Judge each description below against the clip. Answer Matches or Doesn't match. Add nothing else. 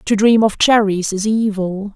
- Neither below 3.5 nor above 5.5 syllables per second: Matches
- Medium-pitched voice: Doesn't match